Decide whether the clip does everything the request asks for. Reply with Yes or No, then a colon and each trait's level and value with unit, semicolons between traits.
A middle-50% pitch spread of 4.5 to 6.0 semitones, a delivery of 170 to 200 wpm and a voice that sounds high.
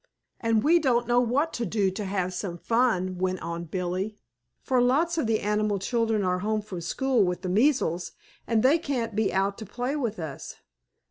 Yes: average, 4.8 semitones; average, 195 wpm; high, 215 Hz